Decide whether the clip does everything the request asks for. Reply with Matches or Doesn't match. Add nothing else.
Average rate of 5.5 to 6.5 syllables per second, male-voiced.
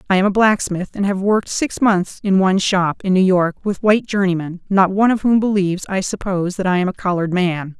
Doesn't match